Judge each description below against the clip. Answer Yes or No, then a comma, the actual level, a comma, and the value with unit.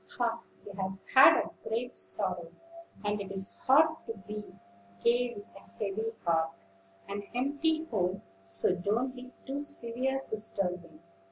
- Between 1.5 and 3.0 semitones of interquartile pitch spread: No, average, 4.8 semitones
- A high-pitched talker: Yes, high, 215 Hz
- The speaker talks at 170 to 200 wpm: No, average, 150 wpm